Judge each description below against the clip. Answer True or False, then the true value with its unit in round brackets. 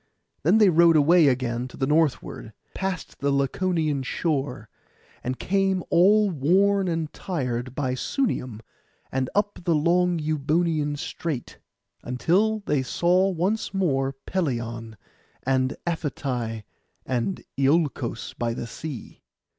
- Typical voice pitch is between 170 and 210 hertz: False (150 Hz)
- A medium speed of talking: False (120 wpm)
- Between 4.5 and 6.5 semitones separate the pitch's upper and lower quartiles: True (5.6 semitones)